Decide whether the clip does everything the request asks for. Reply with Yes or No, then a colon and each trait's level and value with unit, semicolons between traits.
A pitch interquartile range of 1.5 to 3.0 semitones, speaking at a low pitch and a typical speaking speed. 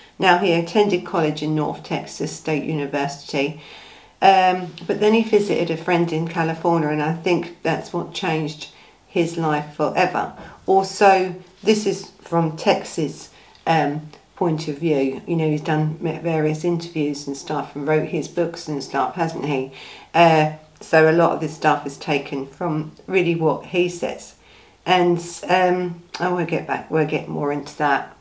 No: average, 2.7 semitones; medium, 165 Hz; average, 160 wpm